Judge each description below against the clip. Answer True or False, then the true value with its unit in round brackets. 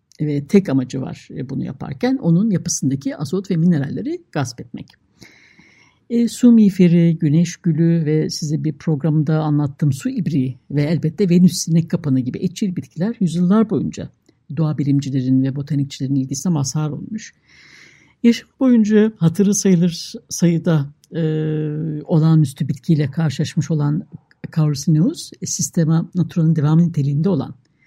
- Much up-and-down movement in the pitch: False (3.3 semitones)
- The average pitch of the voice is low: False (160 Hz)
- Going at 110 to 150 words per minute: True (125 wpm)